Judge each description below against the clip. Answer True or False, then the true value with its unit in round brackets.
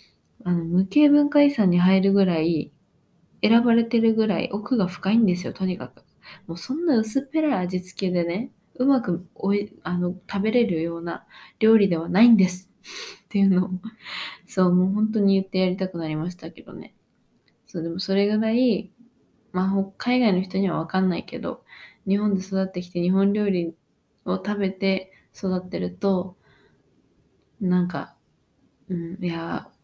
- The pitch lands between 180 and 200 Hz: True (190 Hz)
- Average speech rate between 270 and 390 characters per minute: True (310 characters per minute)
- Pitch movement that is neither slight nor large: True (3.3 semitones)